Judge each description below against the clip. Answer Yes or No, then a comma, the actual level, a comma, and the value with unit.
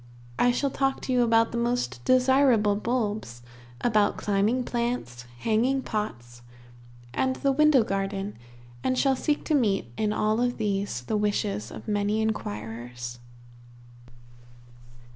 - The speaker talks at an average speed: No, slow, 125 wpm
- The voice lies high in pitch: Yes, high, 215 Hz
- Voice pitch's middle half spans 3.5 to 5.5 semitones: Yes, average, 4.1 semitones